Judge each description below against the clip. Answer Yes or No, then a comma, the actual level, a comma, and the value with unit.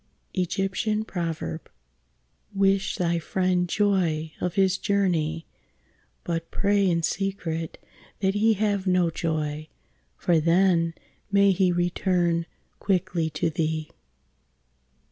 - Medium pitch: Yes, medium, 175 Hz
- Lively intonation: No, average, 2.8 semitones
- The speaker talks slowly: Yes, slow, 95 wpm